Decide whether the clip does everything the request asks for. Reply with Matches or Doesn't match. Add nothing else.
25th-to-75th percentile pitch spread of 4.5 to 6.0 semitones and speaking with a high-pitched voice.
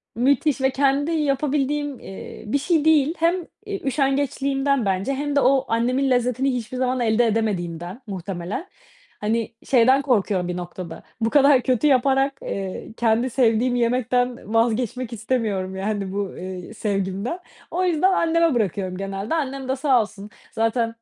Matches